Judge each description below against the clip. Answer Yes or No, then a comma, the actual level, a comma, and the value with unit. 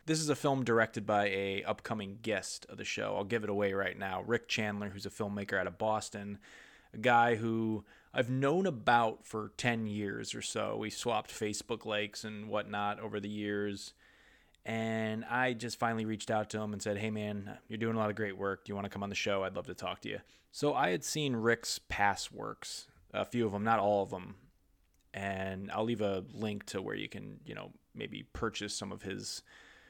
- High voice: No, low, 105 Hz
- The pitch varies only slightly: Yes, narrow, 2.0 semitones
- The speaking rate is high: Yes, fast, 220 wpm